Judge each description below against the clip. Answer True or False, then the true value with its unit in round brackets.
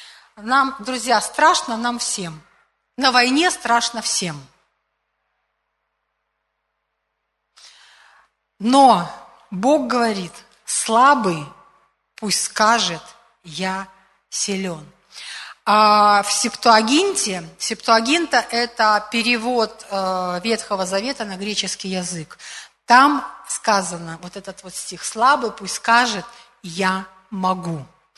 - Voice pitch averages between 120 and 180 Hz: False (215 Hz)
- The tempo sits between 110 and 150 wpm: False (85 wpm)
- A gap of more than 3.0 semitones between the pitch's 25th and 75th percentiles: True (4.2 semitones)